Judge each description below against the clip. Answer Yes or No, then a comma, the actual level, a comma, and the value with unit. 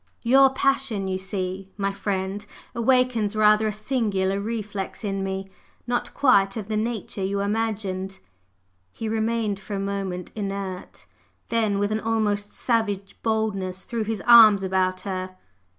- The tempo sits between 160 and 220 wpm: No, average, 140 wpm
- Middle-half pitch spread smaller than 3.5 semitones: Yes, narrow, 2.5 semitones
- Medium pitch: No, high, 205 Hz